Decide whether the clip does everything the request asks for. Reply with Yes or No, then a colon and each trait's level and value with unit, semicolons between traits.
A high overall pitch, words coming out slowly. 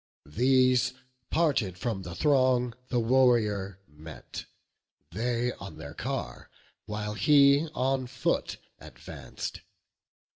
No: low, 120 Hz; slow, 100 wpm